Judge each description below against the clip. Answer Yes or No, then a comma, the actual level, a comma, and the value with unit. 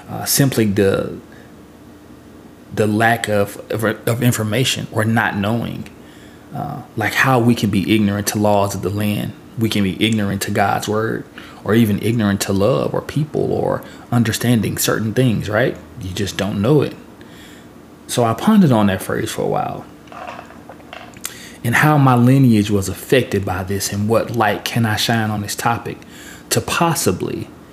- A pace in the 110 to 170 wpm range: Yes, average, 165 wpm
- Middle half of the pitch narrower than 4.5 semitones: Yes, average, 2.9 semitones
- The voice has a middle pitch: No, low, 105 Hz